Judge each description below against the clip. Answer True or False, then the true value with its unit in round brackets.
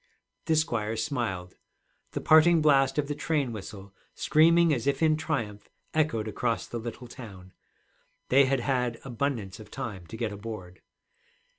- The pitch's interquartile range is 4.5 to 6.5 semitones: True (5.6 semitones)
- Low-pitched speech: True (120 Hz)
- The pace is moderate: True (150 wpm)